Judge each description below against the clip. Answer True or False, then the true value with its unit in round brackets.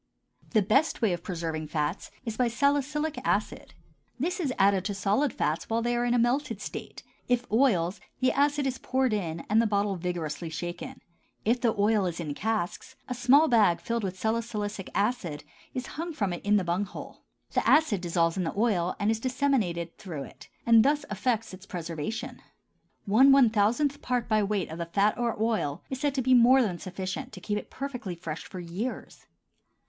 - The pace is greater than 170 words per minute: True (195 wpm)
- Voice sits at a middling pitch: False (215 Hz)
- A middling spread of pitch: False (5.7 semitones)